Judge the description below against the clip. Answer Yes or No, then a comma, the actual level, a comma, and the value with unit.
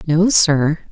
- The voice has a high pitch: No, medium, 165 Hz